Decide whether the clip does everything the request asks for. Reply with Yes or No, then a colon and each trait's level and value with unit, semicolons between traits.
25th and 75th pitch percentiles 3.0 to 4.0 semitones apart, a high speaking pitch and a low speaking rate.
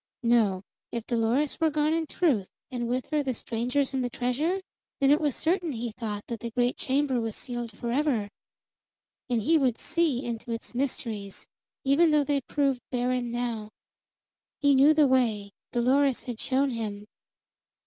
No: average, 3.5 semitones; very high, 250 Hz; average, 165 wpm